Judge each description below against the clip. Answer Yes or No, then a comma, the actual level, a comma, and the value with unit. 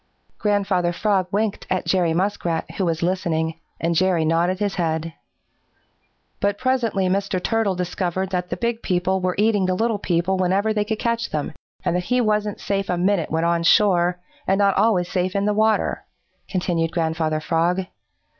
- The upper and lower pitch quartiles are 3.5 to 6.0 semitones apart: No, average, 2.9 semitones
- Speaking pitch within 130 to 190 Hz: Yes, medium, 185 Hz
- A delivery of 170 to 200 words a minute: Yes, average, 175 wpm